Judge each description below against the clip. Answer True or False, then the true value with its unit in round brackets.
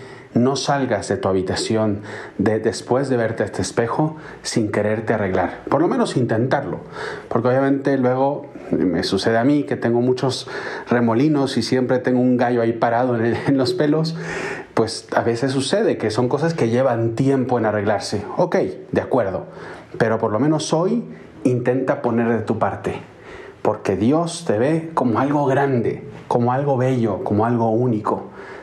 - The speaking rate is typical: True (170 wpm)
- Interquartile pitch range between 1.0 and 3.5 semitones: True (3.2 semitones)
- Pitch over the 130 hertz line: False (125 Hz)